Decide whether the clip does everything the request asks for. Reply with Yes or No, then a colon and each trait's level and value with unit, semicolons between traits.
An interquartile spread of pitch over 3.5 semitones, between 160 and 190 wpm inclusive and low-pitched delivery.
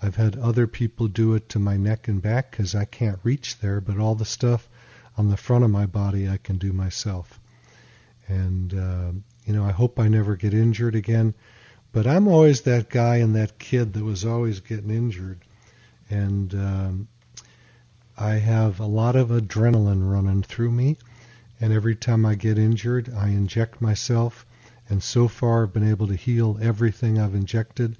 No: narrow, 2.4 semitones; average, 180 wpm; low, 110 Hz